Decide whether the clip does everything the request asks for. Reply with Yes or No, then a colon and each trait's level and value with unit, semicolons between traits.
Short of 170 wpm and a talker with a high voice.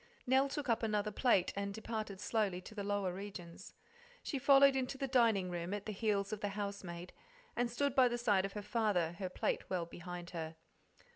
No: average, 200 wpm; high, 205 Hz